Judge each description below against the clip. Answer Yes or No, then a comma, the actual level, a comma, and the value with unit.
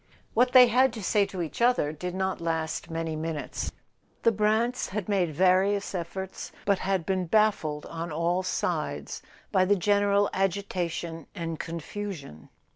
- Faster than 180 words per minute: No, average, 155 wpm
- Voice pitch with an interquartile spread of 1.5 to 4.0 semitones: Yes, average, 3.7 semitones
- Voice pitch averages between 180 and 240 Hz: Yes, medium, 185 Hz